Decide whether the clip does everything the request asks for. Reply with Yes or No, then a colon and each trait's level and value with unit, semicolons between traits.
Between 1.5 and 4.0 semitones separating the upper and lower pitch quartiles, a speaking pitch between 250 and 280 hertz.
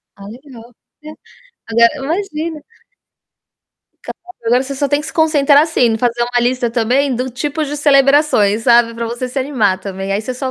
Yes: average, 3.7 semitones; very high, 255 Hz